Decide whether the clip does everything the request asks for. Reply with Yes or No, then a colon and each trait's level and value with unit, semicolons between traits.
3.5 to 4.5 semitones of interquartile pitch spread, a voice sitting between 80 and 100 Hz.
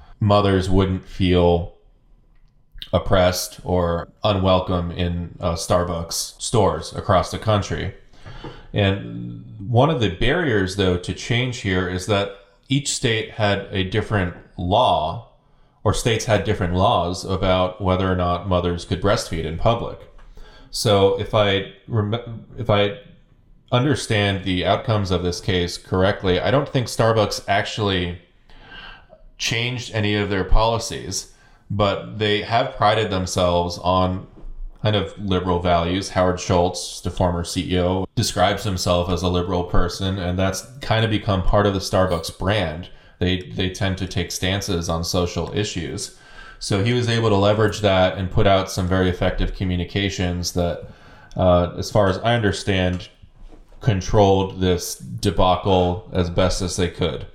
No: narrow, 2.6 semitones; very low, 95 Hz